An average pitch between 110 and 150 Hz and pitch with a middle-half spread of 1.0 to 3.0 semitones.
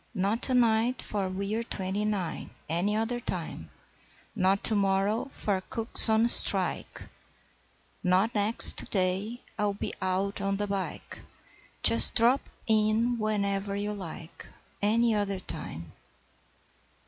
No: high, 205 Hz; narrow, 2.5 semitones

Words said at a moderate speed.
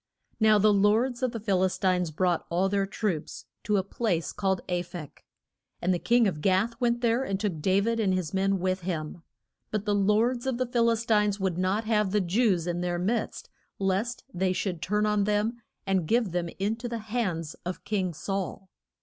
No: fast, 210 wpm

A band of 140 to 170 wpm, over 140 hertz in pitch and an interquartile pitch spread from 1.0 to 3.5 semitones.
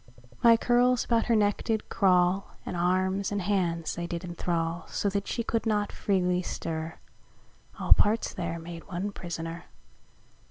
Yes: average, 155 wpm; medium, 185 Hz; average, 3.2 semitones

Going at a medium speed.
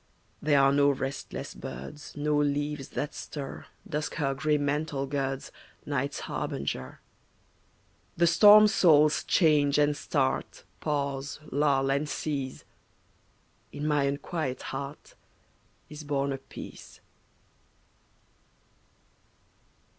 No: slow, 100 wpm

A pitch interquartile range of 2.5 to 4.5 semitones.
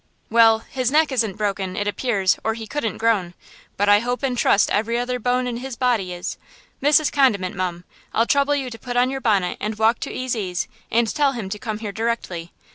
Yes: average, 3.6 semitones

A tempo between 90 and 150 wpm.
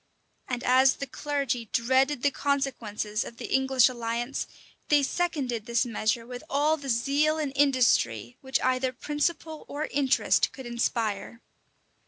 Yes: average, 145 wpm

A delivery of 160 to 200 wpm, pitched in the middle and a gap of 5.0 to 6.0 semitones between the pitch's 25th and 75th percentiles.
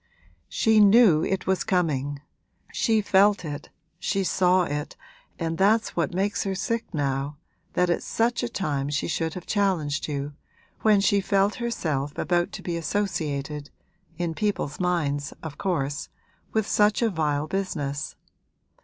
No: average, 145 wpm; medium, 175 Hz; average, 5.3 semitones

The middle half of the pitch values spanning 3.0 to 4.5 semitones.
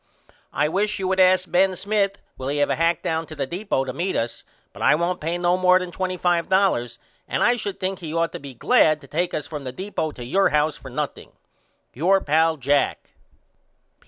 Yes: average, 4.0 semitones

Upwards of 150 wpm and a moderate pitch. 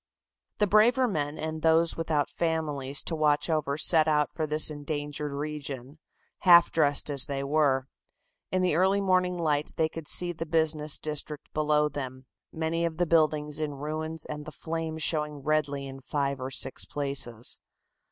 Yes: average, 165 wpm; medium, 155 Hz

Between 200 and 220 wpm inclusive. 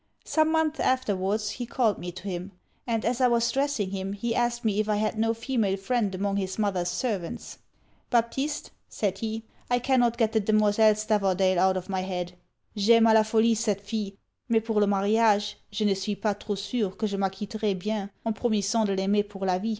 Yes: fast, 205 wpm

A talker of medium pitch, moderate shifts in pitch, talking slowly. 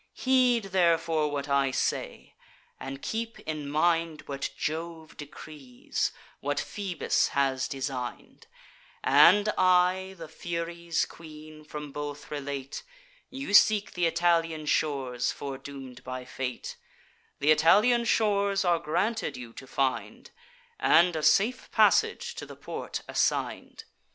Yes: medium, 155 Hz; average, 4.4 semitones; slow, 120 wpm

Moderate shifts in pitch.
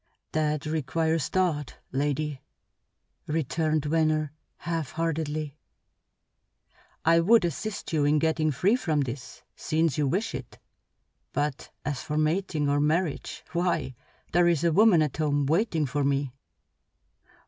No: narrow, 2.3 semitones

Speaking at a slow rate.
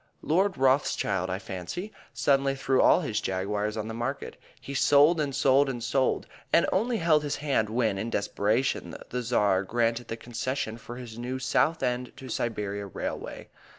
No: average, 165 wpm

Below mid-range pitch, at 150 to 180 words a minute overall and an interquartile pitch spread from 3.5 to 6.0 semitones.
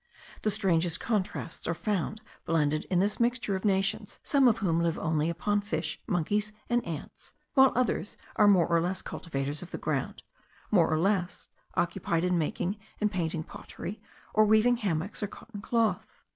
No: high, 190 Hz; average, 170 wpm; average, 4.1 semitones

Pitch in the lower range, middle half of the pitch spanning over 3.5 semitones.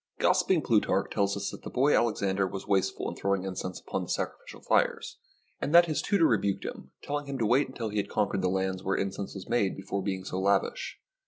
Yes: low, 100 Hz; average, 3.9 semitones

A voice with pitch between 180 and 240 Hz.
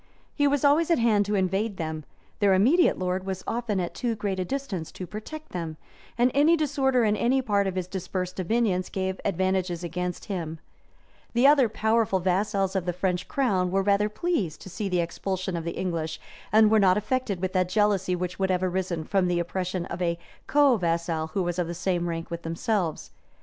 Yes: high, 190 Hz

